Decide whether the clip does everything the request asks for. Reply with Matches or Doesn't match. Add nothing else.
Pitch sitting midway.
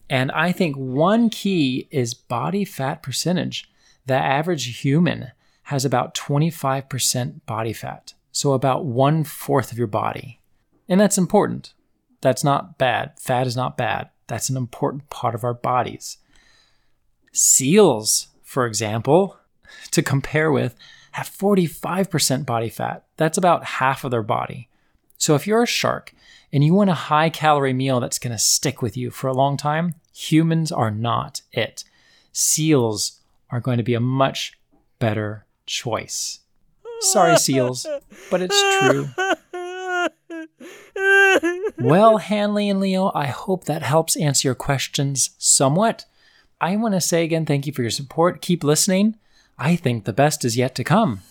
Matches